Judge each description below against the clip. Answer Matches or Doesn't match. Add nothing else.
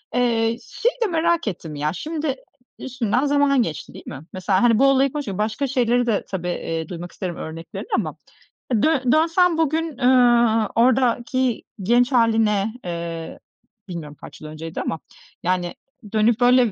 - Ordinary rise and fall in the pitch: Doesn't match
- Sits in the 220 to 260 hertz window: Matches